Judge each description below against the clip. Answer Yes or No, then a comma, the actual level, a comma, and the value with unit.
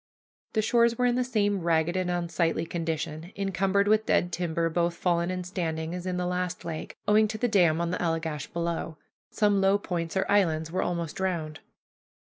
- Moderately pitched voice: Yes, medium, 175 Hz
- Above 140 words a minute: Yes, average, 190 wpm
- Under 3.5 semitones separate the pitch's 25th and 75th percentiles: Yes, average, 3.0 semitones